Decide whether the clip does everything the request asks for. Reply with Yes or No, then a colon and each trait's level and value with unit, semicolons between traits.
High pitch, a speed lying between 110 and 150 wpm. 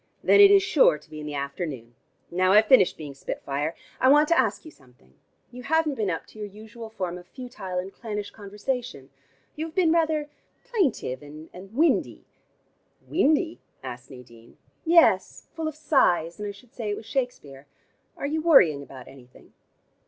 No: high, 210 Hz; average, 180 wpm